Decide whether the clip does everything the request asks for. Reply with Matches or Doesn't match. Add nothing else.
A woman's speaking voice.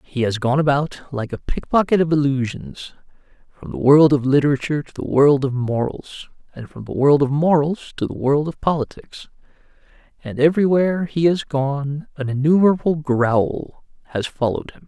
Doesn't match